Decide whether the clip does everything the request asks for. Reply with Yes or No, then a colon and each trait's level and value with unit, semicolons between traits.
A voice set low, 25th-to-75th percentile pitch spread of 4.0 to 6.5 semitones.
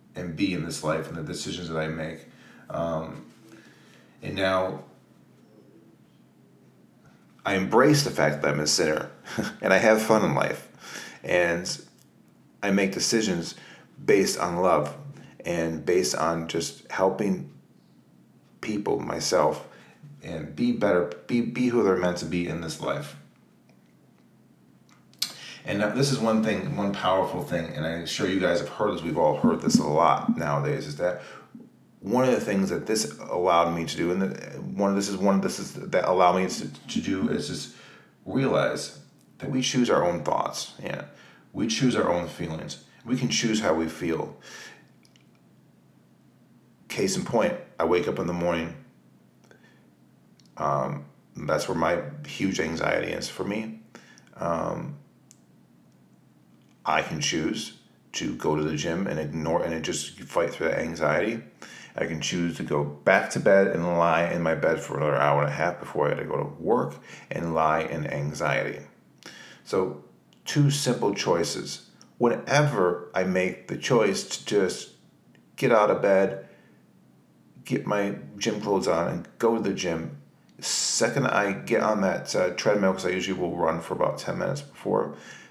Yes: very low, 90 Hz; average, 4.4 semitones